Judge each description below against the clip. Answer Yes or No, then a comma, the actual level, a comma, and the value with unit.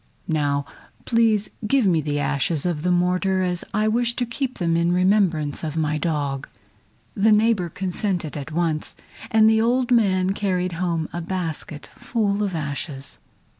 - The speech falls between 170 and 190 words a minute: No, average, 160 wpm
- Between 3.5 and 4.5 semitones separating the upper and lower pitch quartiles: No, average, 5.2 semitones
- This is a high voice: No, medium, 180 Hz